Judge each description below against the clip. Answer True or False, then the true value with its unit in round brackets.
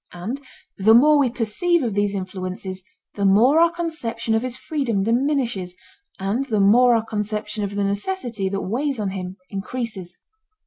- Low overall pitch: False (220 Hz)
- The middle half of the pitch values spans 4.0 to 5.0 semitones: True (4.5 semitones)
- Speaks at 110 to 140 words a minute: False (165 wpm)